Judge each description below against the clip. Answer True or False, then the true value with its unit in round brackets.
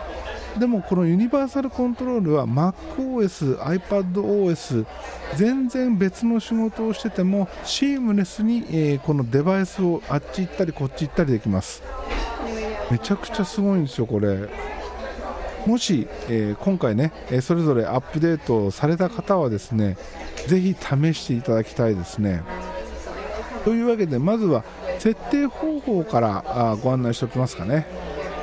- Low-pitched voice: False (175 Hz)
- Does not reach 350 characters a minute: True (310 characters per minute)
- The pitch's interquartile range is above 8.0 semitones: True (8.9 semitones)